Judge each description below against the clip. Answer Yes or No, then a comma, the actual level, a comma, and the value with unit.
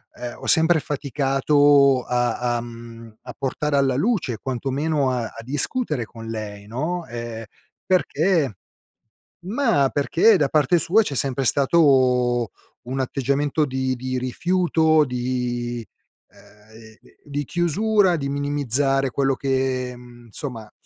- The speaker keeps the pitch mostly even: No, average, 3.6 semitones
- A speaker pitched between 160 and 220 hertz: No, low, 135 Hz